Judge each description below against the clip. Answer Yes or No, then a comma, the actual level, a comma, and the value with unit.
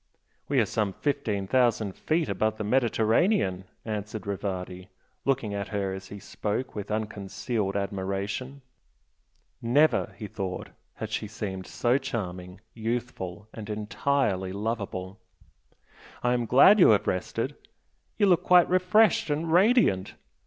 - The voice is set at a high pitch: No, low, 110 Hz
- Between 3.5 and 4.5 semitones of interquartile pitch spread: No, average, 5.0 semitones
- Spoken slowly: Yes, slow, 130 wpm